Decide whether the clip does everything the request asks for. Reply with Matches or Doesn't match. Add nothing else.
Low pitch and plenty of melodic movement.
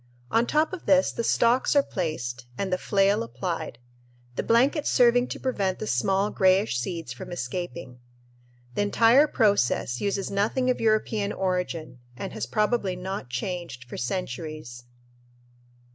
Doesn't match